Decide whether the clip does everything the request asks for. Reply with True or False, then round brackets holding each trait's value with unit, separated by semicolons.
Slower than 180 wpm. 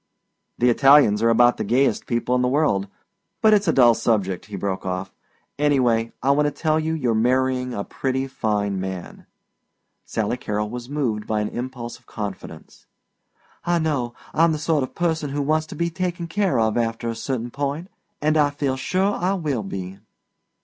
False (185 wpm)